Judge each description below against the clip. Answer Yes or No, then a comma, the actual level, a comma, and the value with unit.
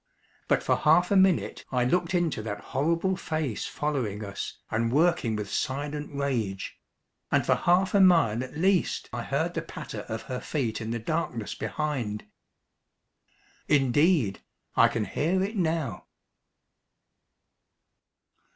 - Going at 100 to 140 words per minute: Yes, slow, 135 wpm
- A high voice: No, medium, 145 Hz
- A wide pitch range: Yes, wide, 7.0 semitones